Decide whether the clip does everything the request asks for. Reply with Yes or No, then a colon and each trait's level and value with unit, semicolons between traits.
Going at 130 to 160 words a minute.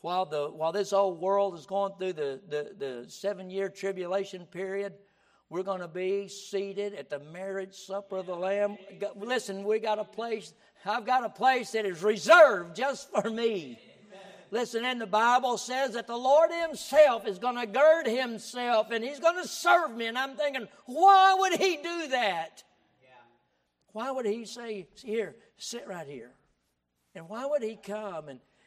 No: average, 180 wpm